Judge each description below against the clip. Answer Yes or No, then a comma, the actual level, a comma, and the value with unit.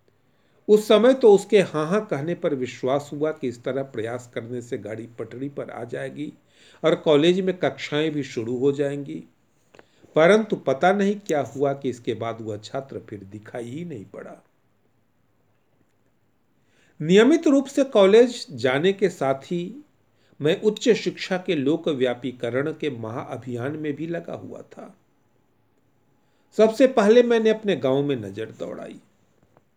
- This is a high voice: No, medium, 150 Hz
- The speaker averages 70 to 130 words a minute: No, average, 145 wpm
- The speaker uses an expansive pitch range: Yes, wide, 7.1 semitones